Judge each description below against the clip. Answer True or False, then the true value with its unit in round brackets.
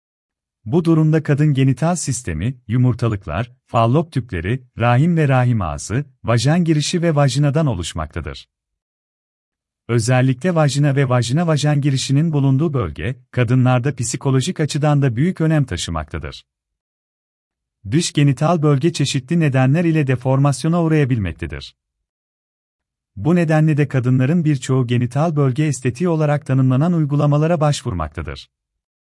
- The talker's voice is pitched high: False (130 Hz)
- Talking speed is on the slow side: False (105 wpm)